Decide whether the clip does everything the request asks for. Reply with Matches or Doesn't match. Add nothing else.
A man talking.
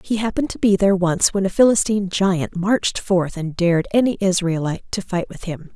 Doesn't match